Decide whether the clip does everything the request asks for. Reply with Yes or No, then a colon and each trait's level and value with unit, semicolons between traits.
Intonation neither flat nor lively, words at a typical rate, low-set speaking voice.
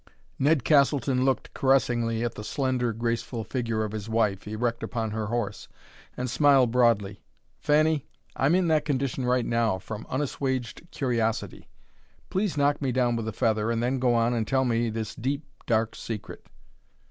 Yes: average, 3.1 semitones; average, 165 wpm; low, 120 Hz